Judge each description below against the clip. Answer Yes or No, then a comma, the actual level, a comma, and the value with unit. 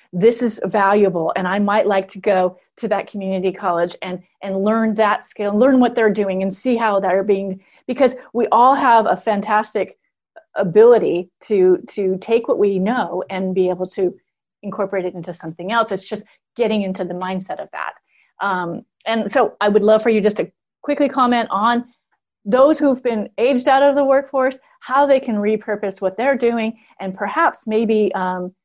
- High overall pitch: Yes, high, 210 Hz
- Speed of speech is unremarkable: Yes, average, 185 wpm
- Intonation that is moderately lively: Yes, average, 3.8 semitones